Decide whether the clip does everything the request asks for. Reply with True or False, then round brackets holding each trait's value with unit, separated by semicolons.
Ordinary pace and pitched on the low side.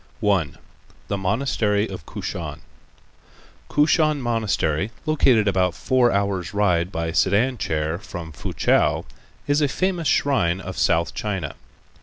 False (120 wpm; 100 Hz)